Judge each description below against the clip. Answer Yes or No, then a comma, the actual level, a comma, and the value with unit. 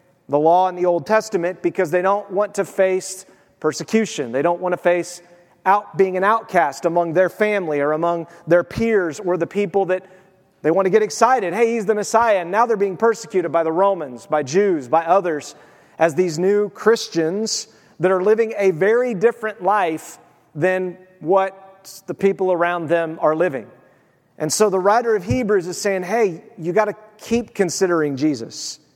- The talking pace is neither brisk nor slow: Yes, average, 180 wpm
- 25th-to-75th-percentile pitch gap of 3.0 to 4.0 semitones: Yes, average, 3.3 semitones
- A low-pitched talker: No, medium, 185 Hz